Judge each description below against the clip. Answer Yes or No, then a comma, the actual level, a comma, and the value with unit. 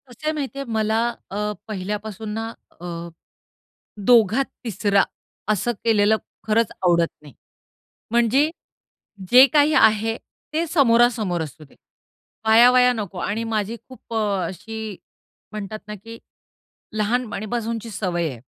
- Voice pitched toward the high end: Yes, high, 220 Hz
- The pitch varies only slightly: No, average, 3.0 semitones